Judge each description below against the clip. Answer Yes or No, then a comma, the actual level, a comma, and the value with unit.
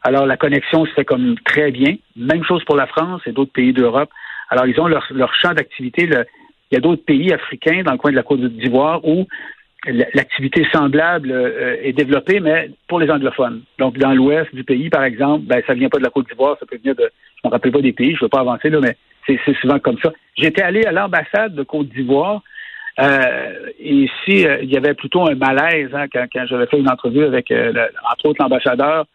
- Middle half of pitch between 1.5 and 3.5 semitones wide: No, average, 4.2 semitones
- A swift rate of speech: Yes, fast, 240 wpm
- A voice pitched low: No, medium, 145 Hz